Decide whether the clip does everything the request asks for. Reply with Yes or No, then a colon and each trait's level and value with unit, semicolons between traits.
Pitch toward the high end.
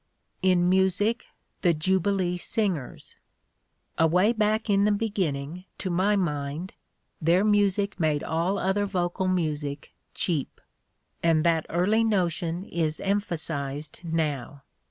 No: medium, 180 Hz